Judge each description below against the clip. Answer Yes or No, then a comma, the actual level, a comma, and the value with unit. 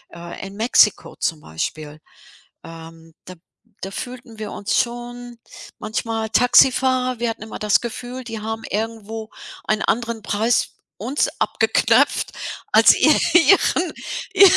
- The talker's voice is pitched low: No, high, 225 Hz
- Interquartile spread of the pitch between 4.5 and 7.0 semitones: No, average, 3.1 semitones